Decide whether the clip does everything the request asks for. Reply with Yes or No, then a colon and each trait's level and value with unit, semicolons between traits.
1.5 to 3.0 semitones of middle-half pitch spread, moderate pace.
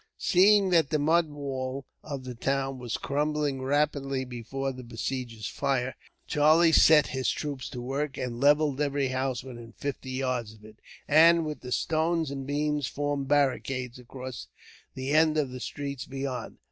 Yes: narrow, 2.5 semitones; average, 160 wpm